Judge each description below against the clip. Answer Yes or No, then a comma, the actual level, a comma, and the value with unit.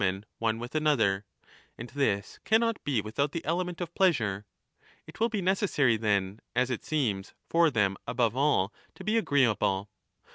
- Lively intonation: Yes, wide, 8.2 semitones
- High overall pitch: No, low, 125 Hz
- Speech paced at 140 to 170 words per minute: No, average, 180 wpm